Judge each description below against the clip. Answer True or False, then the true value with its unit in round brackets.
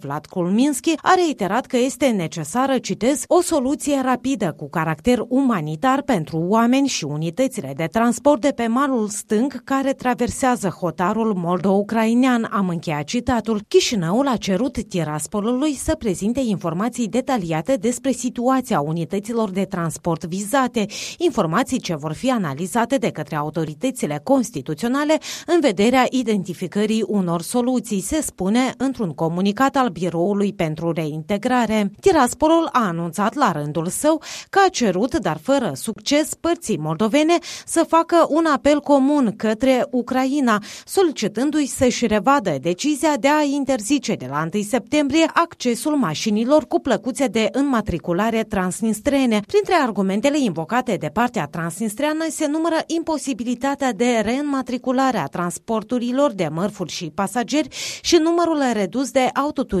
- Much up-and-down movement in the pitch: True (5.9 semitones)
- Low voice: False (240 Hz)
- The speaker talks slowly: False (130 wpm)